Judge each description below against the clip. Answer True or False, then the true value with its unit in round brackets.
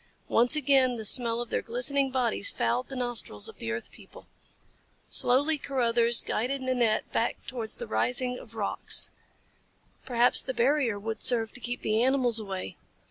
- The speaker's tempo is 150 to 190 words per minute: True (160 wpm)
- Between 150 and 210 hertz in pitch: False (245 Hz)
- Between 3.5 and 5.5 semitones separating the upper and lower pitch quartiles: False (2.4 semitones)